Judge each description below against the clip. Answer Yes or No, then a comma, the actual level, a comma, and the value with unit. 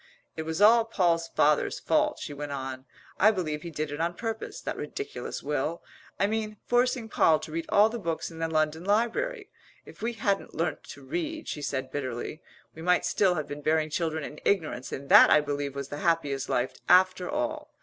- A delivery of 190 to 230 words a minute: Yes, average, 200 wpm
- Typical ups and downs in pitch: No, wide, 6.5 semitones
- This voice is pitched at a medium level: Yes, medium, 165 Hz